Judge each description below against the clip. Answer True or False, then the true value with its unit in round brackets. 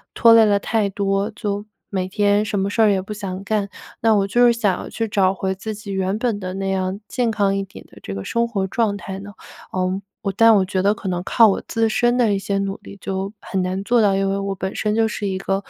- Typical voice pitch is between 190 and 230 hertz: True (200 Hz)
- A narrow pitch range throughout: True (2.0 semitones)